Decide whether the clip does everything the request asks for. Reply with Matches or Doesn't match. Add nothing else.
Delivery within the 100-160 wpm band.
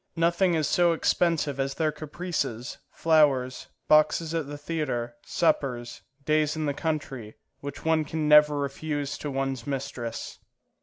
Matches